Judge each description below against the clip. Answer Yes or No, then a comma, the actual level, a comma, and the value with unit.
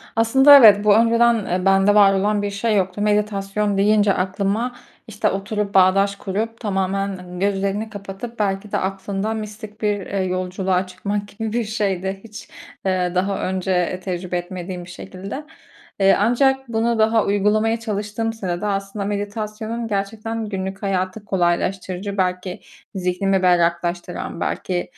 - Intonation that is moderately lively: No, narrow, 2.2 semitones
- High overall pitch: Yes, high, 200 Hz